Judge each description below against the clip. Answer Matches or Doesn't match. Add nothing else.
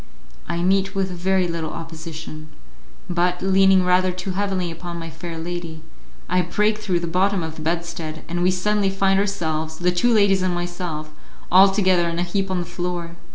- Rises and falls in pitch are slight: Matches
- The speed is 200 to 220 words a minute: Doesn't match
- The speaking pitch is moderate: Matches